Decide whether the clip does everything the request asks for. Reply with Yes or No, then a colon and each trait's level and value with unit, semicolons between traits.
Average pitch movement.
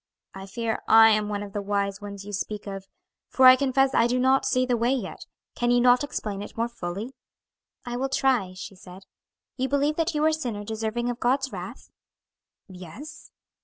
Yes: average, 4.4 semitones